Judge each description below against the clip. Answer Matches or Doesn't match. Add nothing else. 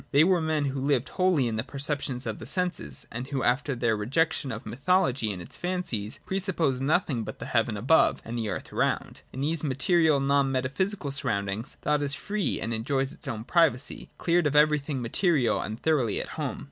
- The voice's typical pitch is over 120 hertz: Matches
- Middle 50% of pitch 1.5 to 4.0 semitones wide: Doesn't match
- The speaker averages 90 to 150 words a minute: Doesn't match